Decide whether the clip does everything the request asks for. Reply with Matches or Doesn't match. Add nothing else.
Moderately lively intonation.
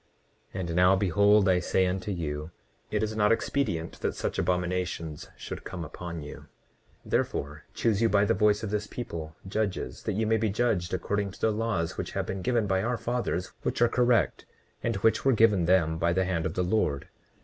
Matches